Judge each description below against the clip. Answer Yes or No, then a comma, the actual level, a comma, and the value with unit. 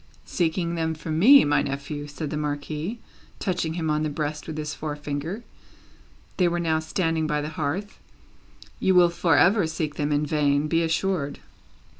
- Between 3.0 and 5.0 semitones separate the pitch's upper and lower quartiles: No, narrow, 2.4 semitones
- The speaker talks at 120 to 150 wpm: No, average, 170 wpm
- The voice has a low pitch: No, medium, 155 Hz